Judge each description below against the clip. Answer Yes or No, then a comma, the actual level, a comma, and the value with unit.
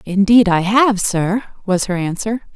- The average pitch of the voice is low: No, high, 200 Hz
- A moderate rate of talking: Yes, average, 165 wpm